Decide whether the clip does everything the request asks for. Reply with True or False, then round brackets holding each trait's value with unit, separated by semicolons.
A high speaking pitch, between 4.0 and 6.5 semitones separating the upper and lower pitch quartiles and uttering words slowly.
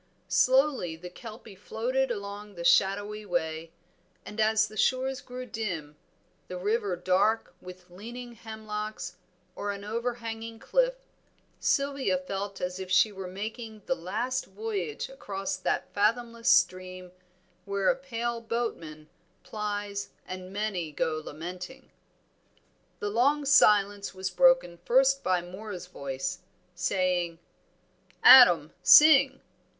True (205 Hz; 4.4 semitones; 120 wpm)